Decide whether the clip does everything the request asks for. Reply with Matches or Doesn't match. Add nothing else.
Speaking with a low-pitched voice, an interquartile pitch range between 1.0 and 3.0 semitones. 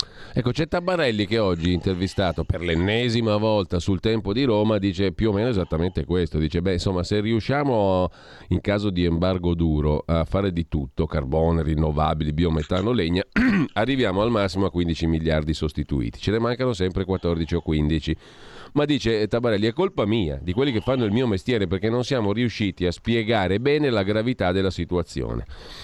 Doesn't match